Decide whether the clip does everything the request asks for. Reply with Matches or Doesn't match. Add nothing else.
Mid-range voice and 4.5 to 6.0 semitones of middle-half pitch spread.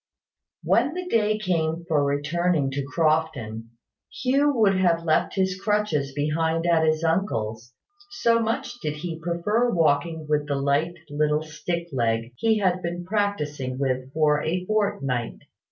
Matches